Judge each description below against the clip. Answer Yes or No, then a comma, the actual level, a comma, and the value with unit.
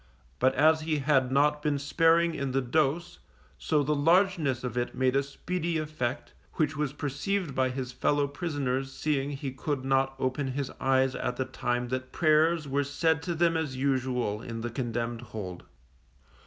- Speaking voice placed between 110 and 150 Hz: Yes, medium, 140 Hz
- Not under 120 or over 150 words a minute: No, average, 175 wpm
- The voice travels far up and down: No, average, 3.0 semitones